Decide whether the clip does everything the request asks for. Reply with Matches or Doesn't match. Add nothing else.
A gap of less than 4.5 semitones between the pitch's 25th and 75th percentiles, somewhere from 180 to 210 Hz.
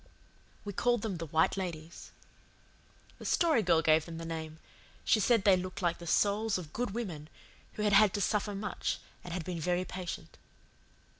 Matches